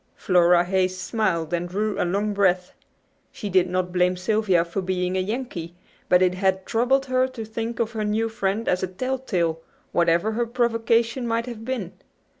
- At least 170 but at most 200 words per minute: Yes, average, 180 wpm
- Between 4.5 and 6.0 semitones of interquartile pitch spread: No, average, 4.0 semitones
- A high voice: Yes, high, 195 Hz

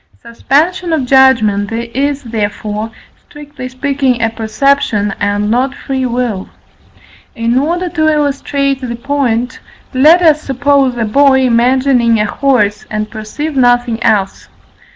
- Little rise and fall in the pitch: No, average, 3.8 semitones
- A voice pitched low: No, very high, 255 Hz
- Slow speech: Yes, slow, 125 wpm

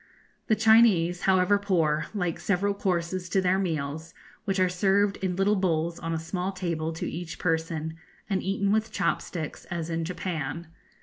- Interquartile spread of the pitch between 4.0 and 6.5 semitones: No, average, 3.0 semitones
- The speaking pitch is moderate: Yes, medium, 180 Hz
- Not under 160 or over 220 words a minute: Yes, average, 170 wpm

